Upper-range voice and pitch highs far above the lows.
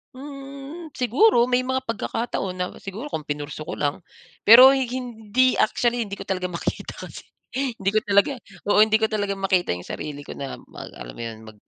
Yes: high, 220 Hz; wide, 6.1 semitones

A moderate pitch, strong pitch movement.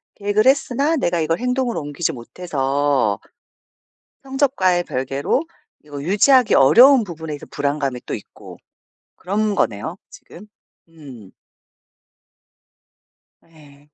Yes: medium, 165 Hz; wide, 7.3 semitones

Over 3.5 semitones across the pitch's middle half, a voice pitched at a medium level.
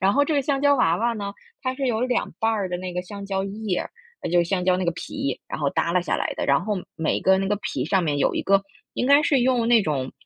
No: average, 5.1 semitones; high, 195 Hz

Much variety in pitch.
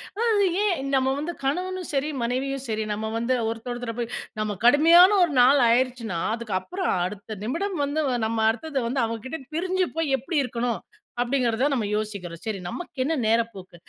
Yes: wide, 5.8 semitones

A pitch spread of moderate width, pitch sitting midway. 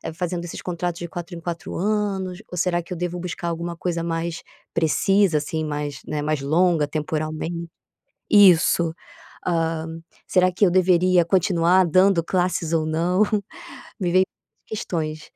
No: narrow, 2.0 semitones; medium, 170 Hz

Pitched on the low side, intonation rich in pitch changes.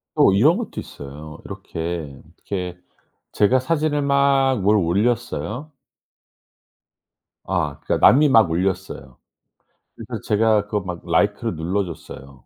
Yes: low, 100 Hz; wide, 6.6 semitones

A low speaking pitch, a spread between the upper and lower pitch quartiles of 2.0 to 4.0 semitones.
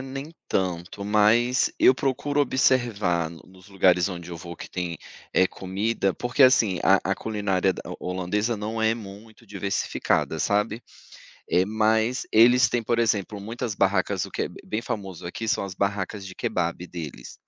Yes: low, 105 Hz; average, 3.6 semitones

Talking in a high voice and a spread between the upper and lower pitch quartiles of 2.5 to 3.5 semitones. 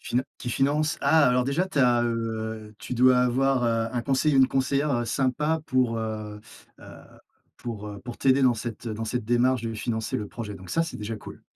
No: low, 120 Hz; average, 3.1 semitones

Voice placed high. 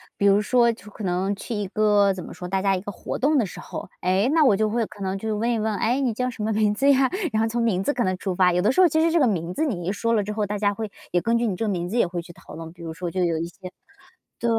Yes: high, 210 Hz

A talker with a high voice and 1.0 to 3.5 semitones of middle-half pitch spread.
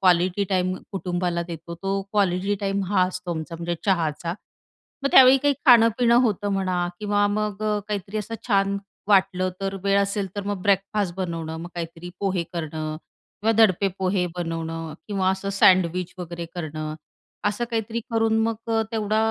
Yes: high, 195 Hz; average, 3.1 semitones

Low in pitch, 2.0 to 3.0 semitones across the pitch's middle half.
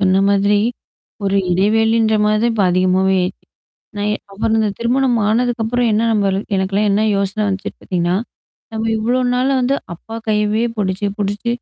No: high, 210 Hz; narrow, 2.5 semitones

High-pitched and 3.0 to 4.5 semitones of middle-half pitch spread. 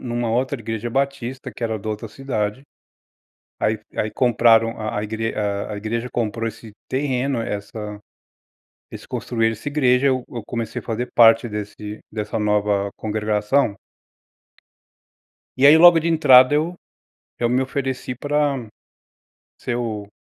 No: low, 115 Hz; average, 3.5 semitones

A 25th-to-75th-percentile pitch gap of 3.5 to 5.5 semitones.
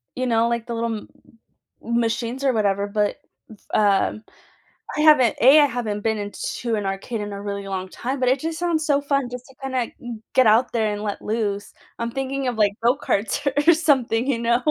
Yes: average, 3.8 semitones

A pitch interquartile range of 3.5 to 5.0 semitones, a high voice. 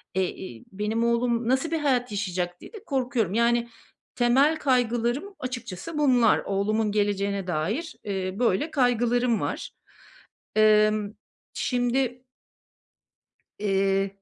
Yes: average, 3.9 semitones; high, 230 Hz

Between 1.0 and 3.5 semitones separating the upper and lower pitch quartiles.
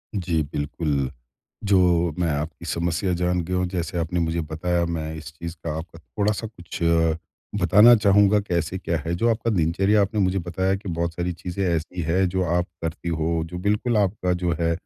Yes: narrow, 2.5 semitones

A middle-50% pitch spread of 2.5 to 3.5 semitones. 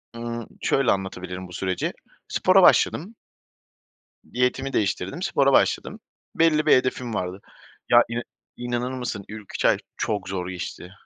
No: average, 5.3 semitones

